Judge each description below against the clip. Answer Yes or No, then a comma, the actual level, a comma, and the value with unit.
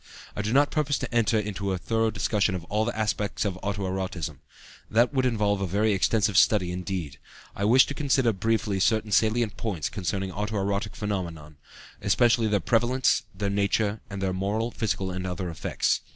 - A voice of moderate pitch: No, low, 105 Hz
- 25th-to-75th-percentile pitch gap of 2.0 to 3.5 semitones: Yes, average, 2.8 semitones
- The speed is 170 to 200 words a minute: Yes, average, 180 wpm